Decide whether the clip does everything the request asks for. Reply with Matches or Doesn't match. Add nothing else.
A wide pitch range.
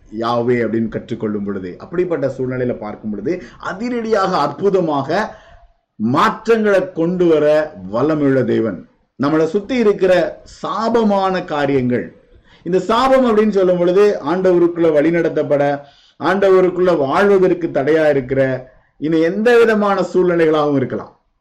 Matches